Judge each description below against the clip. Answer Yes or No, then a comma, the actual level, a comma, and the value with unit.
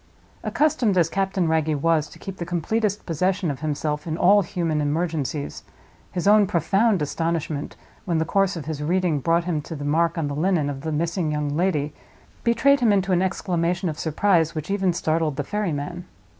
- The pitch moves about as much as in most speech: Yes, average, 3.7 semitones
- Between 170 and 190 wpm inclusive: Yes, average, 185 wpm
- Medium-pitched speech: Yes, medium, 170 Hz